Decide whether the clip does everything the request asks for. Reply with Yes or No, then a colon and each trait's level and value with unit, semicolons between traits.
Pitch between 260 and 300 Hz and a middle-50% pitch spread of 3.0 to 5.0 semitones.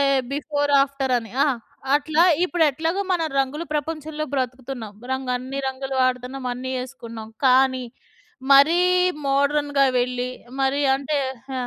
No: very high, 270 Hz; narrow, 2.4 semitones